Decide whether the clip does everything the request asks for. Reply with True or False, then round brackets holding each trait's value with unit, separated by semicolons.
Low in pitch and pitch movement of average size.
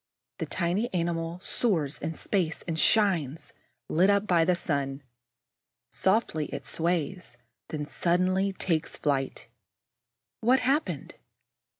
False (170 Hz; 3.5 semitones)